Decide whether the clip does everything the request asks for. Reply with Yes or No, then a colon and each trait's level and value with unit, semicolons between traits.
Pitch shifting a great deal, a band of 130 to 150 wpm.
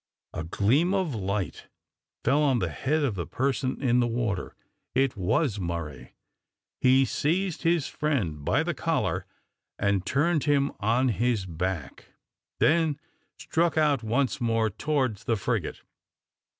Yes: wide, 6.7 semitones; slow, 135 wpm